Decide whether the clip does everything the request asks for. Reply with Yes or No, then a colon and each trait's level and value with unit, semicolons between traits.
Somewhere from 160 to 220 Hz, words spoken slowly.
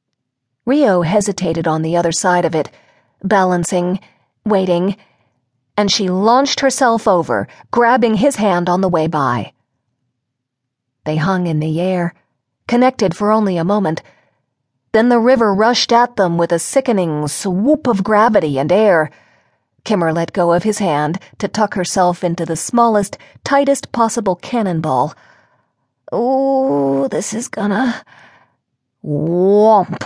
Yes: high, 190 Hz; slow, 130 wpm